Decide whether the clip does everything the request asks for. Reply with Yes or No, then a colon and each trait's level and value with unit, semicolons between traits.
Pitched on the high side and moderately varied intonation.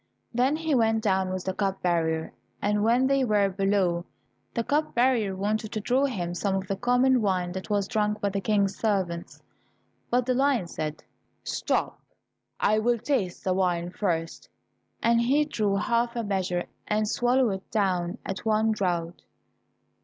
Yes: high, 205 Hz; average, 4.1 semitones